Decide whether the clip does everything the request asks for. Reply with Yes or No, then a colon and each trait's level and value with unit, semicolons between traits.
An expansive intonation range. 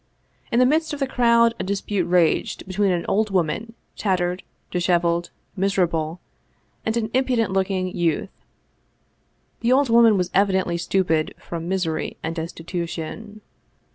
No: average, 4.4 semitones